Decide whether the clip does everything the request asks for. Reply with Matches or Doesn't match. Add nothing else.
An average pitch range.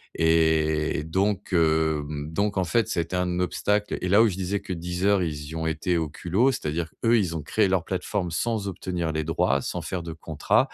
Matches